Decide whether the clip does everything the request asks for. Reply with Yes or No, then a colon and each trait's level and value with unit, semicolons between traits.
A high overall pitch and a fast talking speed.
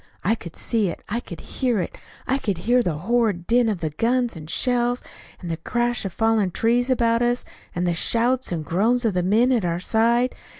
Yes: high, 225 Hz; fast, 215 wpm